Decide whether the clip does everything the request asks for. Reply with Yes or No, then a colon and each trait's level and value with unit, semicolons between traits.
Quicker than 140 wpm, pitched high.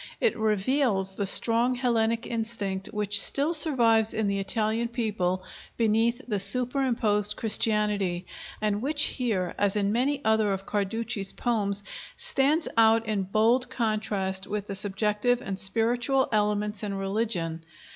No: slow, 135 wpm; high, 215 Hz